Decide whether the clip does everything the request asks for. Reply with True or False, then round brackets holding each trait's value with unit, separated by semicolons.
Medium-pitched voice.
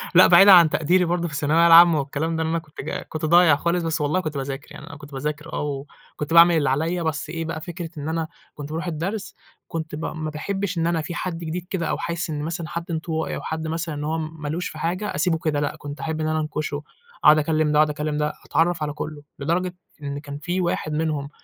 True (160 Hz)